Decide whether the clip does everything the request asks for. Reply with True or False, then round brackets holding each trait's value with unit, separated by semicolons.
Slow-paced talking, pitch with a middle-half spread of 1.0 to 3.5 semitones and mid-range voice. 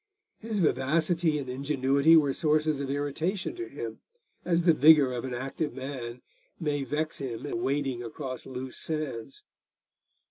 False (145 wpm; 3.2 semitones; 145 Hz)